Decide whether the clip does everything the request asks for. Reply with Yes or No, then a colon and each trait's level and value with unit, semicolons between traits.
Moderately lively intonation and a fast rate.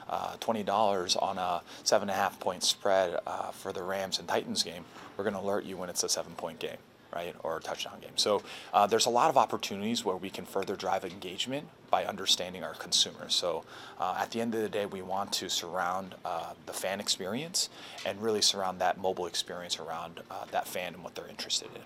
Yes: average, 3.2 semitones; fast, 220 wpm